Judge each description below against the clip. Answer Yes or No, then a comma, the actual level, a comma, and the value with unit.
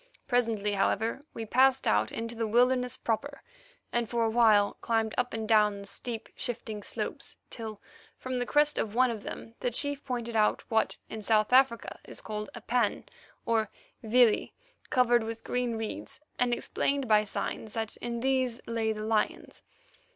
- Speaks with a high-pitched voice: Yes, high, 230 Hz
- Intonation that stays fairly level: Yes, narrow, 2.2 semitones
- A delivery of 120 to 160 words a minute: No, average, 170 wpm